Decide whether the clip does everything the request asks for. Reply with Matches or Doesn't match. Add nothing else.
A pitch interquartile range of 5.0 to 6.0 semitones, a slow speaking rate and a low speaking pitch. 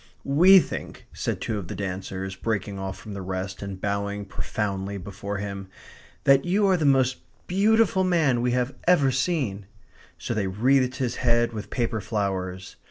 Doesn't match